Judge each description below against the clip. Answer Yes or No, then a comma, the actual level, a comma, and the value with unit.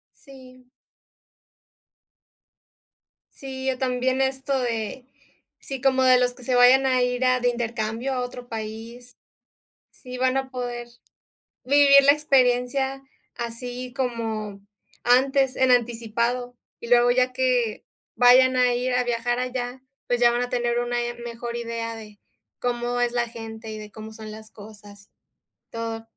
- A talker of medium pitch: No, high, 245 Hz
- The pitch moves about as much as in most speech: No, narrow, 1.6 semitones